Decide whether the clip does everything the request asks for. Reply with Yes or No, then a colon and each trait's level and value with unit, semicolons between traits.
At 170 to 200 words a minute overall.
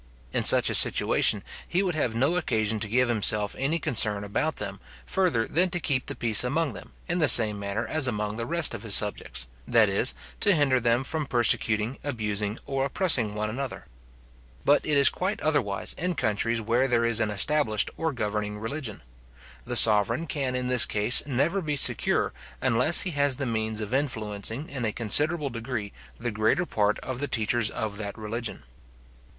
Yes: average, 185 wpm